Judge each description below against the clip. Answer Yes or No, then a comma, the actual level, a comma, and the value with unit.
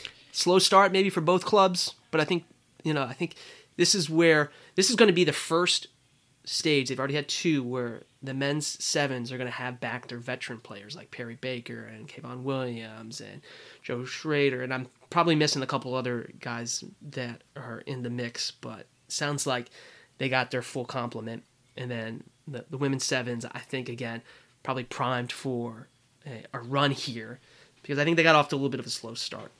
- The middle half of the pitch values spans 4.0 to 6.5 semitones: No, average, 3.3 semitones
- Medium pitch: No, low, 130 Hz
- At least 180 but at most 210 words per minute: Yes, fast, 205 wpm